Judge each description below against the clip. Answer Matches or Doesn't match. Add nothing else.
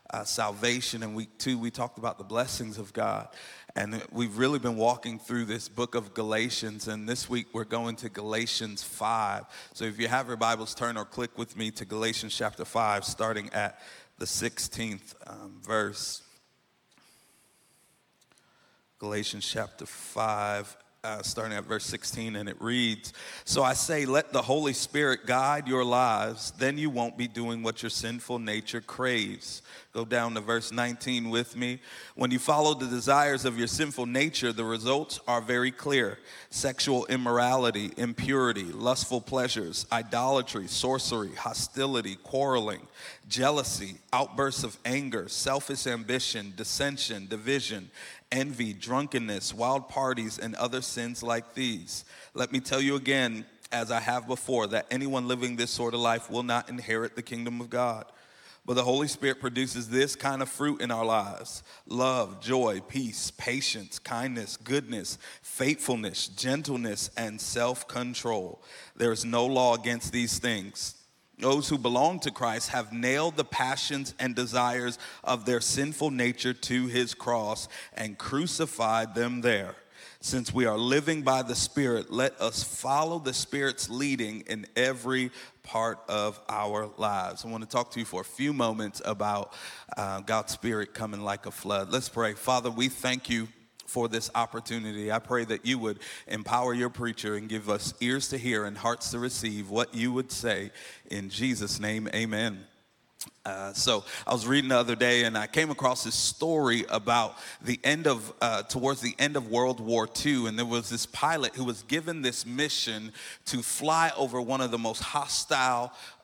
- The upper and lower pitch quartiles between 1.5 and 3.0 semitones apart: Matches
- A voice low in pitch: Matches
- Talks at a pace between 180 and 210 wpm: Doesn't match